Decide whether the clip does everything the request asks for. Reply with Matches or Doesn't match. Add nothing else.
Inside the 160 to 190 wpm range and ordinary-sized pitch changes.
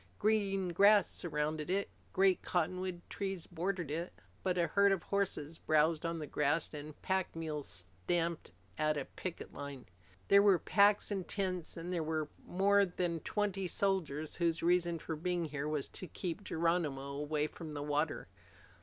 Matches